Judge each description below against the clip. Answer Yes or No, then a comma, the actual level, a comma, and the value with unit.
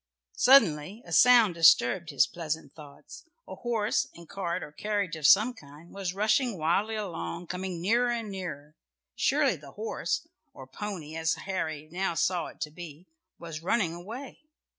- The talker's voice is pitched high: No, medium, 175 Hz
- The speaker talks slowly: No, average, 160 wpm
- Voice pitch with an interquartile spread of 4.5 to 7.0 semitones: Yes, average, 4.8 semitones